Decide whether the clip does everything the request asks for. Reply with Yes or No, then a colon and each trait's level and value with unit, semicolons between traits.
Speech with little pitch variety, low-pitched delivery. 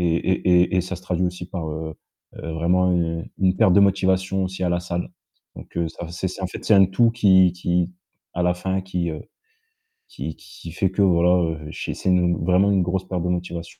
Yes: narrow, 1.5 semitones; very low, 90 Hz